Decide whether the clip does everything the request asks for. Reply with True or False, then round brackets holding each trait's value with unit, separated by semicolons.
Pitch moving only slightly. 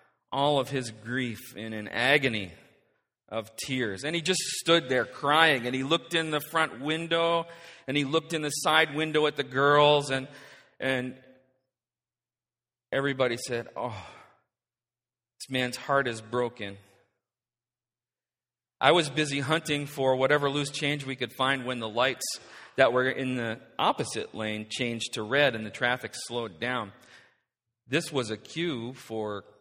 False (3.5 semitones)